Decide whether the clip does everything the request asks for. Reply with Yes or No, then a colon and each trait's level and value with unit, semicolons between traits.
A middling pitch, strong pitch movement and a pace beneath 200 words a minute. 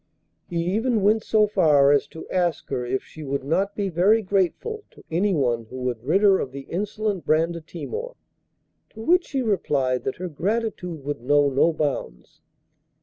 Yes: medium, 170 Hz; wide, 6.7 semitones; average, 170 wpm